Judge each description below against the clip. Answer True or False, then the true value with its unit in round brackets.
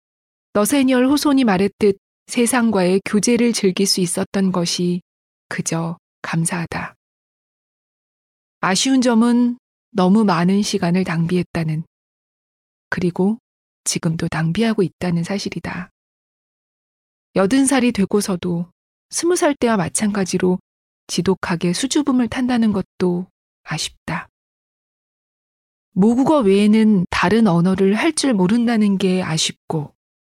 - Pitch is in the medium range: False (195 Hz)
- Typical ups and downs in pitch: True (4.5 semitones)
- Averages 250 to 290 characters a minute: False (235 characters per minute)